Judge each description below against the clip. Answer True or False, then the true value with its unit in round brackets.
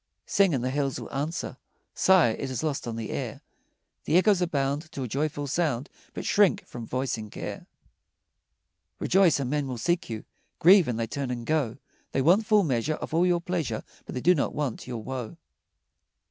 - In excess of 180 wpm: True (190 wpm)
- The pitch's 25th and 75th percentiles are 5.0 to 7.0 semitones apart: True (5.5 semitones)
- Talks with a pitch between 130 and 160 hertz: True (140 Hz)